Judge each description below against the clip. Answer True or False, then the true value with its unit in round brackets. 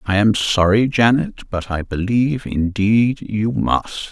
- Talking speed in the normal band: True (145 wpm)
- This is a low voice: True (110 Hz)